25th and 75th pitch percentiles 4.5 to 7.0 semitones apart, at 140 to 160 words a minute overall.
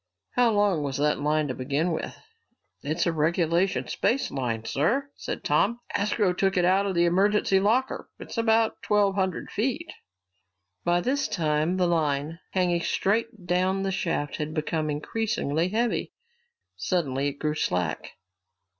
Yes: average, 5.2 semitones; average, 150 wpm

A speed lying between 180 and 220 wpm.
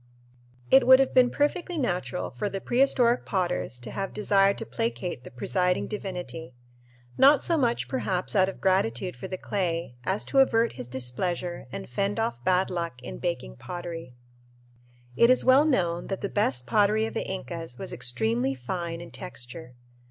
No: average, 170 wpm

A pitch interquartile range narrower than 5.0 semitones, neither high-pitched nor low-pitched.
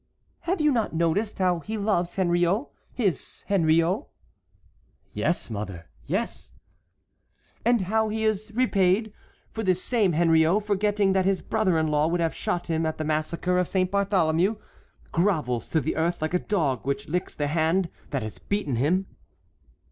Yes: average, 4.2 semitones; medium, 180 Hz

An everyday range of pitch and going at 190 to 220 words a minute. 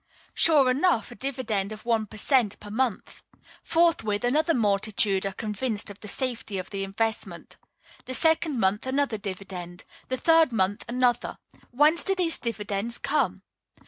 No: average, 4.7 semitones; average, 150 wpm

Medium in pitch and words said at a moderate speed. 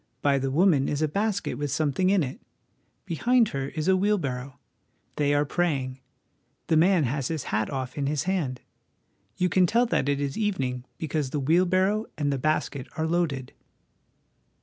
Yes: medium, 150 Hz; average, 175 wpm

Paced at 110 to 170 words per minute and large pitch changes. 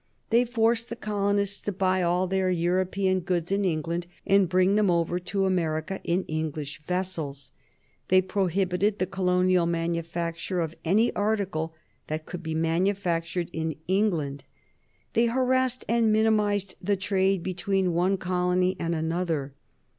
No: average, 140 wpm; average, 3.0 semitones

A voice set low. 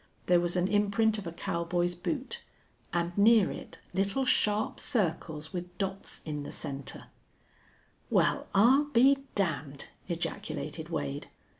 No: high, 190 Hz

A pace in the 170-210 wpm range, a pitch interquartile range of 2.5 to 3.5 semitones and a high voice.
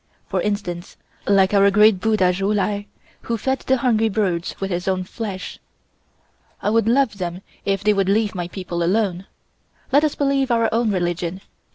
Yes: average, 175 wpm; average, 3.2 semitones; high, 200 Hz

